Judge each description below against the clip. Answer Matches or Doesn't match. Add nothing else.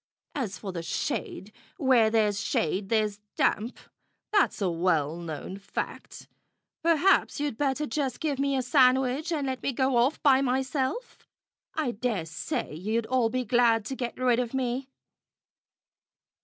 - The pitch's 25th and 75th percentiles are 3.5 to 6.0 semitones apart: Matches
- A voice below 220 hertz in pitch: Doesn't match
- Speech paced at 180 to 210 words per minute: Doesn't match